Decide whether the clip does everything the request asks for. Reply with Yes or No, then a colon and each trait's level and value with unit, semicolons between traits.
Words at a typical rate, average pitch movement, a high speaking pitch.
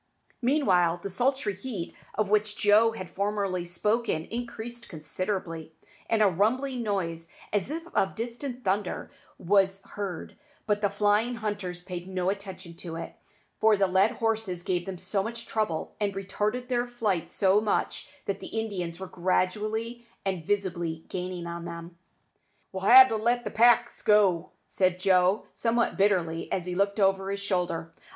Yes: average, 160 wpm; average, 3.4 semitones; high, 200 Hz